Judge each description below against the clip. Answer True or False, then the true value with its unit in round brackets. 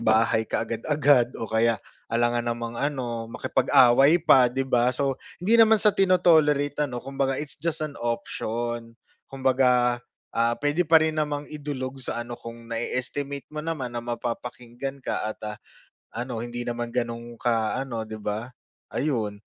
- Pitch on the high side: False (125 Hz)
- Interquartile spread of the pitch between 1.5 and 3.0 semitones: False (3.5 semitones)